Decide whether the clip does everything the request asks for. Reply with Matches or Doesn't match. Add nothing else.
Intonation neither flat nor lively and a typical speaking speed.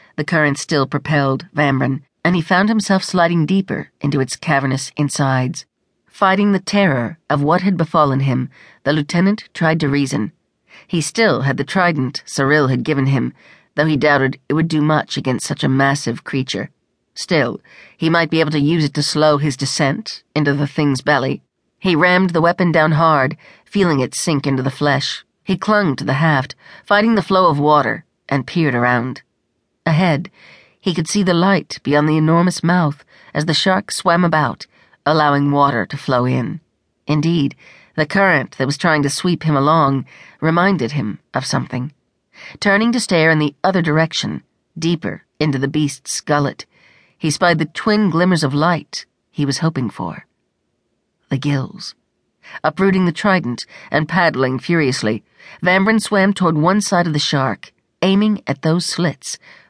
Matches